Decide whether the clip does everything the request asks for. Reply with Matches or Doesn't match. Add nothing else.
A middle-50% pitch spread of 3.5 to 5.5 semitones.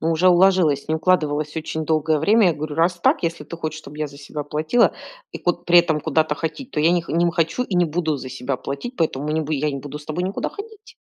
Doesn't match